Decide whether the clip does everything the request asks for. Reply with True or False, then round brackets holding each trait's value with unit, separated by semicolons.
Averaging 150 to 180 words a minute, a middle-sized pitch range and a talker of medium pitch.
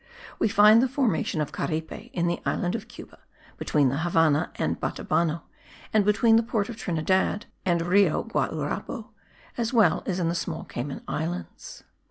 True (160 wpm; 5.0 semitones; 180 Hz)